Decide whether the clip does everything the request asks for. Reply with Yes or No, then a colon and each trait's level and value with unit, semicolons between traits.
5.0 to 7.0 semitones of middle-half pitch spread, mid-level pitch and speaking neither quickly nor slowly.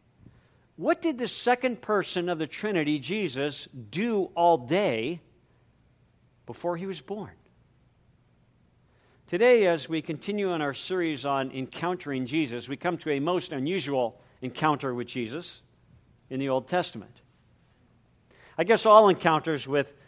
No: wide, 5.5 semitones; medium, 160 Hz; slow, 130 wpm